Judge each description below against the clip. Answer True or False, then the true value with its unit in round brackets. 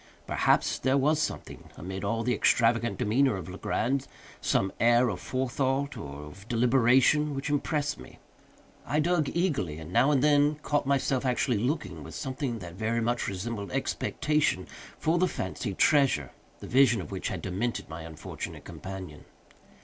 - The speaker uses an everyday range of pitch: False (6.3 semitones)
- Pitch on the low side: True (120 Hz)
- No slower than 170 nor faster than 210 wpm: False (155 wpm)